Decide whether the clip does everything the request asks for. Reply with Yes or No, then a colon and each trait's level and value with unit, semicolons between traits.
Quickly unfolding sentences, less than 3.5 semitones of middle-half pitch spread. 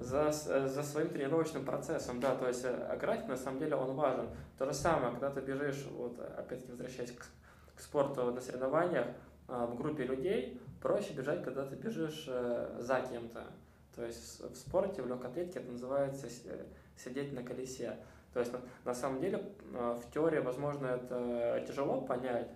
Yes: fast, 170 wpm; narrow, 2.4 semitones